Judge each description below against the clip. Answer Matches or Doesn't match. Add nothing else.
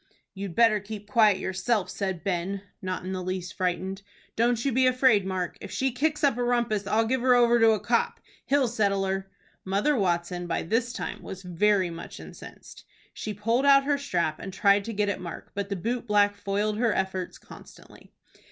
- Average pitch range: Matches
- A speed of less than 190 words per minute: Doesn't match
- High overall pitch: Matches